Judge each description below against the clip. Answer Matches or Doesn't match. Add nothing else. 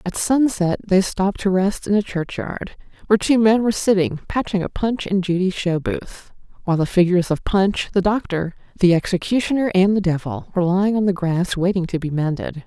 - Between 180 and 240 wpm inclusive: Matches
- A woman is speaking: Matches